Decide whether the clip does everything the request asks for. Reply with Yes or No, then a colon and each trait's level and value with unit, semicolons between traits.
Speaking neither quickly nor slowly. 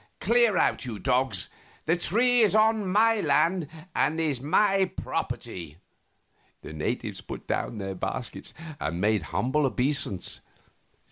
No: slow, 130 wpm